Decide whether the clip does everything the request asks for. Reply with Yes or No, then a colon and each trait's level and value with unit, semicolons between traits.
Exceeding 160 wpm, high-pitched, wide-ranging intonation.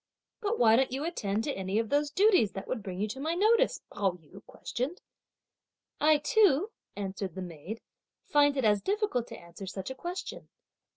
Yes: average, 185 wpm; very high, 255 Hz; wide, 8.9 semitones